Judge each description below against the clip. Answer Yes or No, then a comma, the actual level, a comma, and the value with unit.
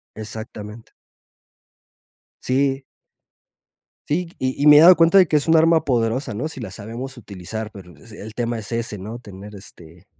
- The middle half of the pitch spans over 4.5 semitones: Yes, average, 5.2 semitones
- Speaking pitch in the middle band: No, low, 115 Hz